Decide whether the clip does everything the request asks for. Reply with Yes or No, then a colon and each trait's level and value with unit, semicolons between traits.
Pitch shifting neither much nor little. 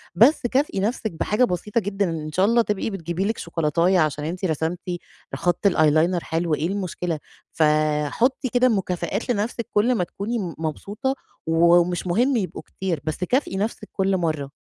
Yes: average, 4.7 semitones